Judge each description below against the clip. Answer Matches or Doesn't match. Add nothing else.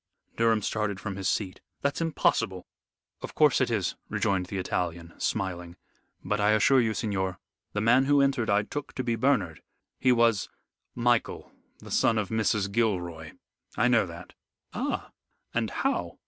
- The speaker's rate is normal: Matches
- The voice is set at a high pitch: Doesn't match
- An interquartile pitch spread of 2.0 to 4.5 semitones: Matches